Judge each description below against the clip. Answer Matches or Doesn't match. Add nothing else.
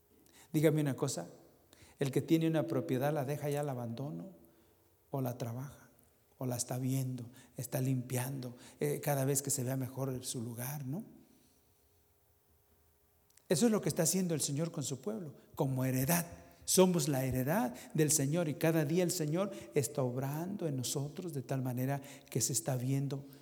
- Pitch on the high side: Doesn't match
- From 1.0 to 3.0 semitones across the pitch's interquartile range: Doesn't match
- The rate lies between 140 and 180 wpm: Matches